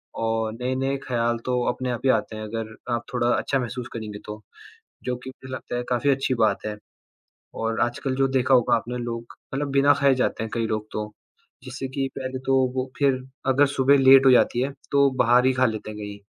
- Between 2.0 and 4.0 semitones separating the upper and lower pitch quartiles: Yes, average, 2.8 semitones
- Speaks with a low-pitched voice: Yes, low, 125 Hz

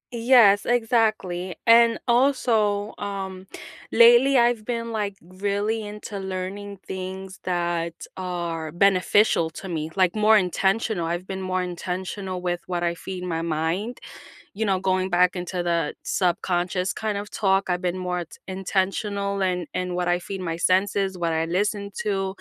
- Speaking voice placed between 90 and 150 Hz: No, high, 190 Hz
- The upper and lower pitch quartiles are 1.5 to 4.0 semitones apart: Yes, narrow, 2.5 semitones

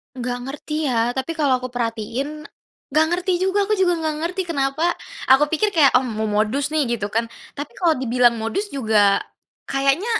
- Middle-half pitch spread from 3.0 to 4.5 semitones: No, average, 5.3 semitones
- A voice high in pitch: Yes, very high, 275 Hz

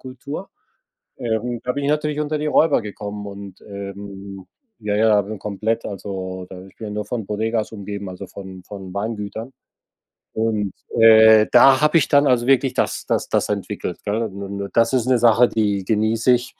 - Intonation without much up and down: No, average, 3.3 semitones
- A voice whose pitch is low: Yes, low, 110 Hz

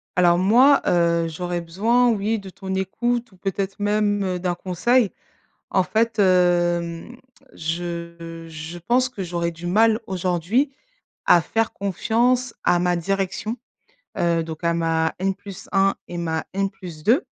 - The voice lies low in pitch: No, medium, 185 Hz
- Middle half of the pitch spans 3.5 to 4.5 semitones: Yes, average, 4.0 semitones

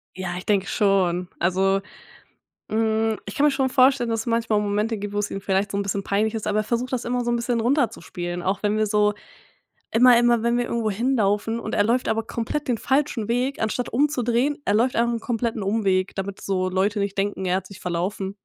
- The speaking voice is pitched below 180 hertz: No, high, 215 Hz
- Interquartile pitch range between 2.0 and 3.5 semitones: Yes, average, 3.2 semitones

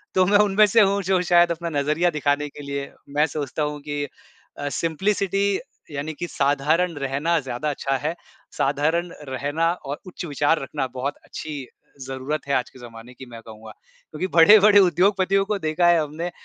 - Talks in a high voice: No, medium, 155 Hz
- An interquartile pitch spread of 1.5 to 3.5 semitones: No, average, 4.1 semitones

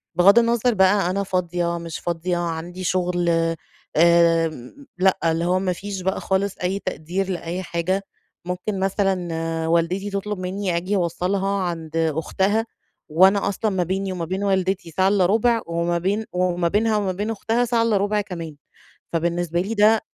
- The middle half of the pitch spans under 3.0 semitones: Yes, narrow, 2.6 semitones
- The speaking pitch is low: No, medium, 185 Hz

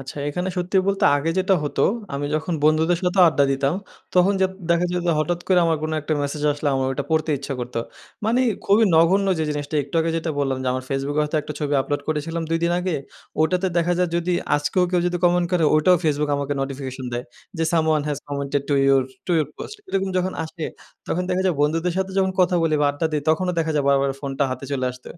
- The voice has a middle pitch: Yes, medium, 155 Hz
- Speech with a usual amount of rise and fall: Yes, average, 3.8 semitones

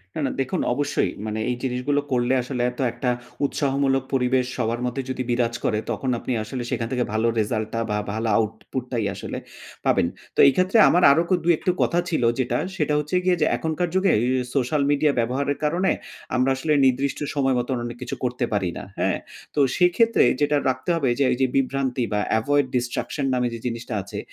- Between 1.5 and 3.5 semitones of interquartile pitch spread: Yes, average, 3.1 semitones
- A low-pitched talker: Yes, low, 130 Hz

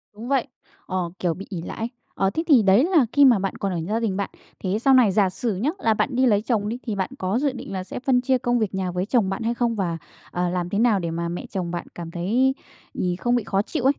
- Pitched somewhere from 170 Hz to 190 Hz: No, high, 205 Hz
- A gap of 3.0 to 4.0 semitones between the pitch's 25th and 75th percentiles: No, average, 4.8 semitones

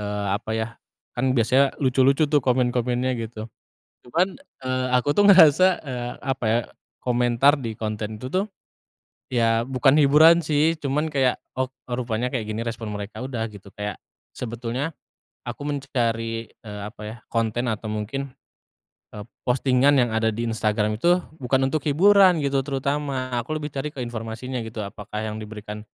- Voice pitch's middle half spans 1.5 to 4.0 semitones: Yes, average, 3.7 semitones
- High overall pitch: No, low, 125 Hz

